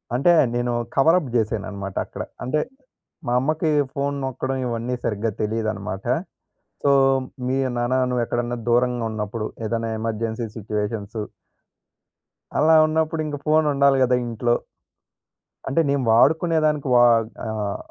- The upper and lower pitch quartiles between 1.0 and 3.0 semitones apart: No, average, 4.1 semitones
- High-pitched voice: No, low, 120 Hz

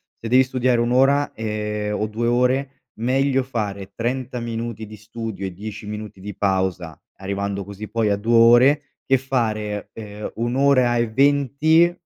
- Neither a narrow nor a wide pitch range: Yes, average, 3.6 semitones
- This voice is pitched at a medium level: No, low, 115 Hz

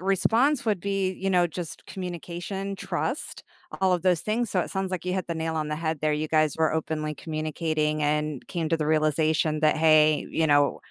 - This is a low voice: No, medium, 160 Hz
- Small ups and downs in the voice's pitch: No, average, 3.2 semitones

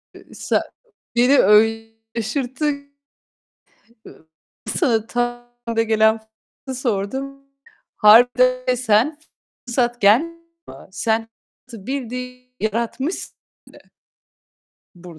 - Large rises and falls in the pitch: No, average, 2.8 semitones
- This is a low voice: No, high, 240 Hz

